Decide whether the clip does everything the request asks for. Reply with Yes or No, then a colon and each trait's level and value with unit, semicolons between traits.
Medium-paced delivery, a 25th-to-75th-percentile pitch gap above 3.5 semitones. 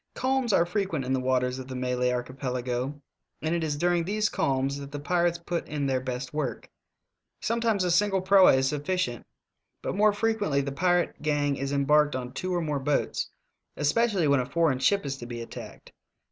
Yes: average, 190 wpm; wide, 5.5 semitones